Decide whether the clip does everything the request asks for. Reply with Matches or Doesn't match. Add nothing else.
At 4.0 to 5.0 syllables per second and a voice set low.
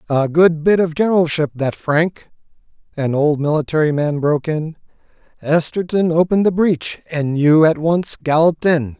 Doesn't match